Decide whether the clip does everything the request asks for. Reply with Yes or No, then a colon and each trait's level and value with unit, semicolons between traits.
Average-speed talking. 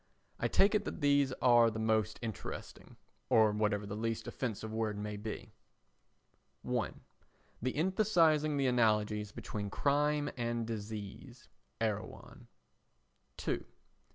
No: slow, 115 wpm